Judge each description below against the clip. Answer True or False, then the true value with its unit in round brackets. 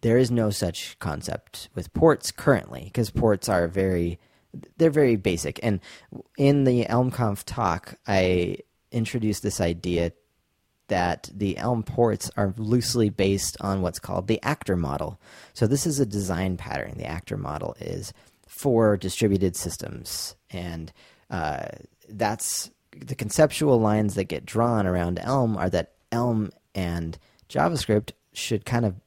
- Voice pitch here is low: True (105 Hz)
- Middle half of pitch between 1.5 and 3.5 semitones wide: False (4.5 semitones)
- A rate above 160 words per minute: False (140 wpm)